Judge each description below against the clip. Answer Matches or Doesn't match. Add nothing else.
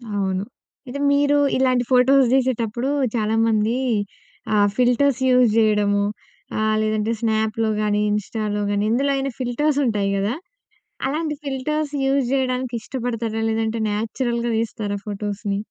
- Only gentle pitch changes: Doesn't match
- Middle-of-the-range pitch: Doesn't match